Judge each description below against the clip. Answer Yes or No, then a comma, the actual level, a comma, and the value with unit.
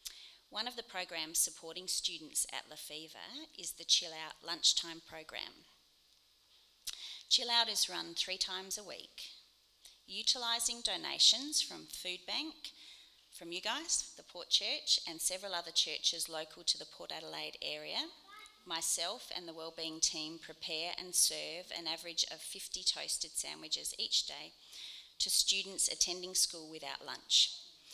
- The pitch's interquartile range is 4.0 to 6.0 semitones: Yes, average, 4.4 semitones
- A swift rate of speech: No, average, 140 wpm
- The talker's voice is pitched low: No, medium, 175 Hz